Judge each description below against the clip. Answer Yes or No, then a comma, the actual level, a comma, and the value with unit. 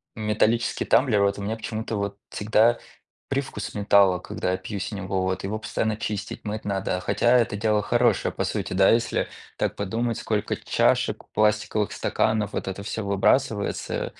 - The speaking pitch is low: Yes, low, 105 Hz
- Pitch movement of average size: No, narrow, 1.9 semitones